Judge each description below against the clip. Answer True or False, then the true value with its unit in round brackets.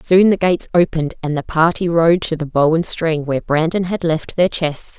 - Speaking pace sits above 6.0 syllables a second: False (5.2 syllables/s)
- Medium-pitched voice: True (165 Hz)